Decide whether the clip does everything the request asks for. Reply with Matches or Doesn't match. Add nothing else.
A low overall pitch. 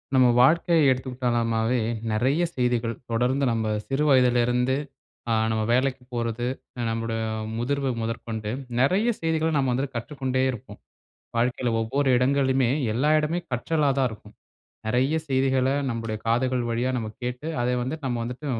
Matches